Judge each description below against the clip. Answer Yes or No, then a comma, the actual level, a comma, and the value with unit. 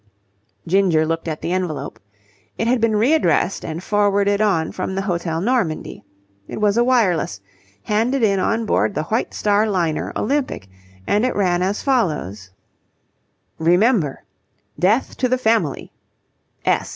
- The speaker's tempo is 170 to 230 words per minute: No, average, 140 wpm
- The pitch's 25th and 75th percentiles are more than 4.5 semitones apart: Yes, average, 5.0 semitones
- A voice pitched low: No, high, 200 Hz